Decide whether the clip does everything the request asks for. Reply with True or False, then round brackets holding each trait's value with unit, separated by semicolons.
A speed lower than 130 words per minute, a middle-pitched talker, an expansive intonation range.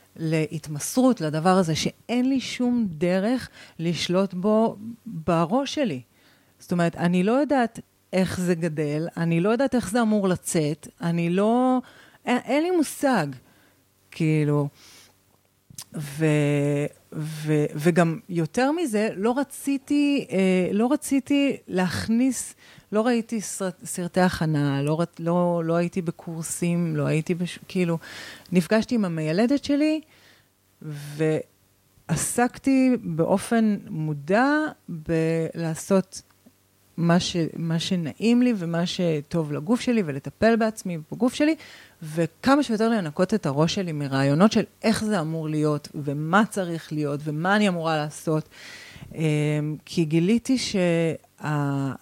True (115 wpm; 175 Hz; 6.3 semitones)